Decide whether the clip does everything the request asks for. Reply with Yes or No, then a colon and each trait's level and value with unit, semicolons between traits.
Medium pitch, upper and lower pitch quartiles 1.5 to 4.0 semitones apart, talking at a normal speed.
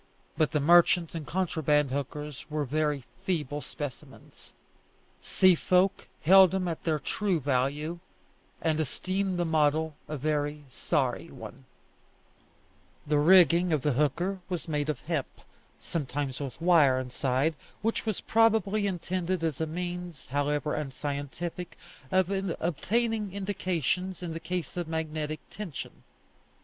No: medium, 160 Hz; average, 3.7 semitones; slow, 130 wpm